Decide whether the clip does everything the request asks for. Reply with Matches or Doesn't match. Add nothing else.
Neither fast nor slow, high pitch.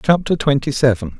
Doesn't match